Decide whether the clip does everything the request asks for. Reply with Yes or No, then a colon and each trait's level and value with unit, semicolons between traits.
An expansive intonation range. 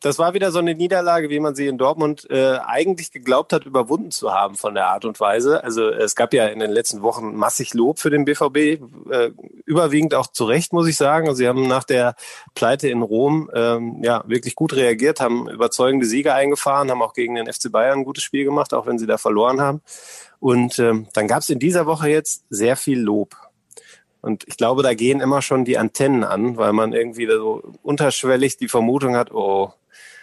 No: average, 4.7 semitones